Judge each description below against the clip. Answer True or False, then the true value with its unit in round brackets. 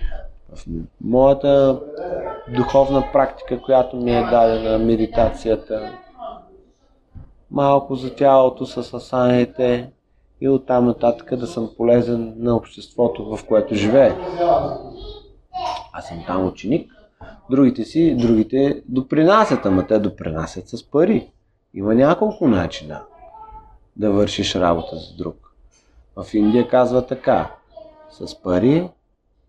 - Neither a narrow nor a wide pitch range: True (3.8 semitones)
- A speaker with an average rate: False (105 wpm)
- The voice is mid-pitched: False (125 Hz)